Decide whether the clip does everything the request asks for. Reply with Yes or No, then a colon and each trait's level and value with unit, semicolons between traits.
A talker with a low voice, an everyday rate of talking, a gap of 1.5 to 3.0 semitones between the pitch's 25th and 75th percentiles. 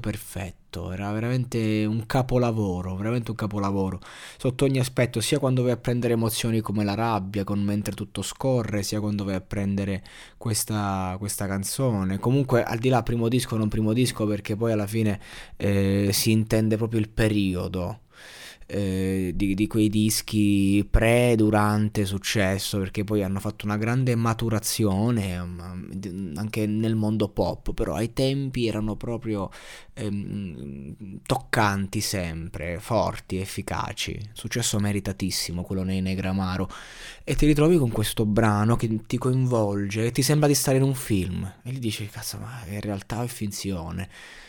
Yes: low, 105 Hz; average, 150 wpm; average, 2.7 semitones